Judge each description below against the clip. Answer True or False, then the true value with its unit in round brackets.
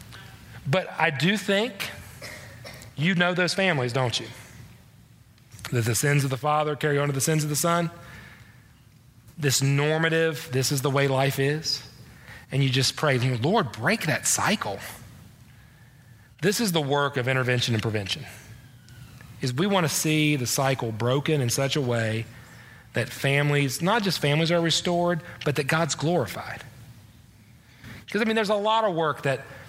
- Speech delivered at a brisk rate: False (160 wpm)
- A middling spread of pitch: True (4.4 semitones)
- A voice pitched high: False (135 Hz)